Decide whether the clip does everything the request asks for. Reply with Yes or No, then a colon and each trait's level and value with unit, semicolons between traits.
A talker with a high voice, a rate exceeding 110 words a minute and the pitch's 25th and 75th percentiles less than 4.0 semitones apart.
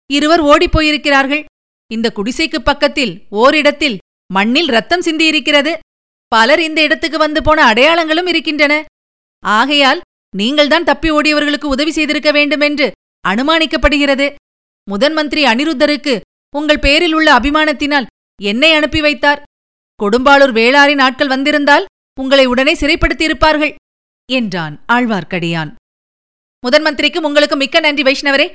No: very high, 295 Hz; average, 100 wpm; average, 2.7 semitones